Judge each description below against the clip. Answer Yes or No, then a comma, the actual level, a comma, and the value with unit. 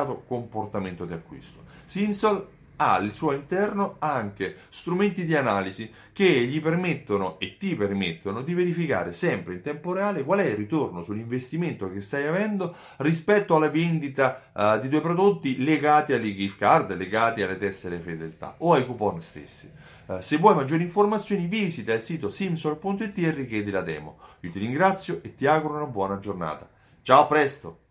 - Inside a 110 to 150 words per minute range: No, average, 160 wpm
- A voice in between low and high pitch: Yes, medium, 145 Hz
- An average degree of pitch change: No, wide, 9.0 semitones